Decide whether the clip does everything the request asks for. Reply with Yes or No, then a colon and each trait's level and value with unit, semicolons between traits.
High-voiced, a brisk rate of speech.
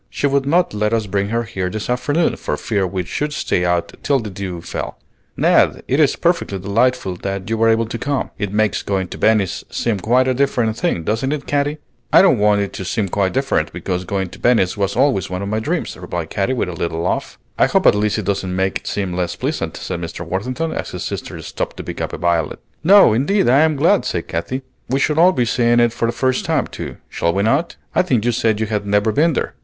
No: low, 110 Hz; fast, 245 wpm